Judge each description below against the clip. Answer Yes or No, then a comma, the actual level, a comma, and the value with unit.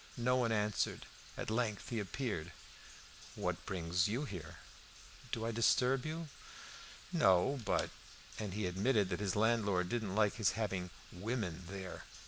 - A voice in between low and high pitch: No, low, 105 Hz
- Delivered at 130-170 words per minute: Yes, average, 145 wpm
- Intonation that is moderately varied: Yes, average, 4.1 semitones